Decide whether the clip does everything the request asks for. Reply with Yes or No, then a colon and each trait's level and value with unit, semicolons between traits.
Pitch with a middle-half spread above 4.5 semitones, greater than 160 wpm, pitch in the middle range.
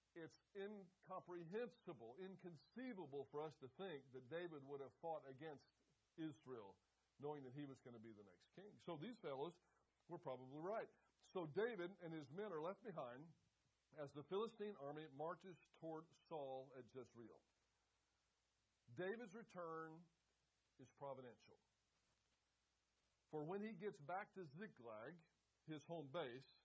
No: average, 5.2 semitones; slow, 135 wpm; medium, 155 Hz